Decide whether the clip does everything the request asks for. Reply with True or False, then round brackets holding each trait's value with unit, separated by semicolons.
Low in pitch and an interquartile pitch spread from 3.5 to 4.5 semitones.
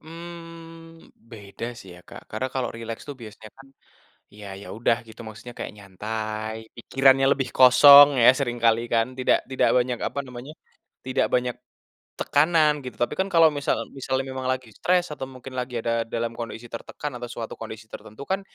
True (125 Hz; 3.8 semitones)